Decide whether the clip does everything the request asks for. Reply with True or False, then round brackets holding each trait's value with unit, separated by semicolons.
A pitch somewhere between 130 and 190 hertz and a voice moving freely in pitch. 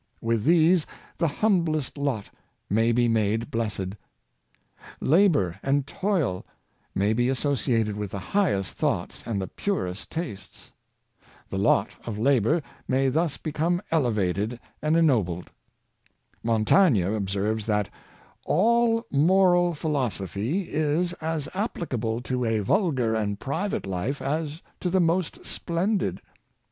True (135 Hz; 7.7 semitones)